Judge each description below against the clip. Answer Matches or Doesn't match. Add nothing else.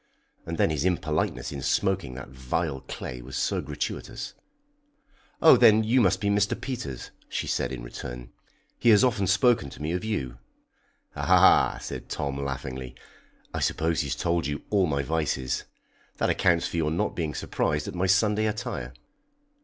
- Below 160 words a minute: Doesn't match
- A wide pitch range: Matches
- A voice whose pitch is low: Matches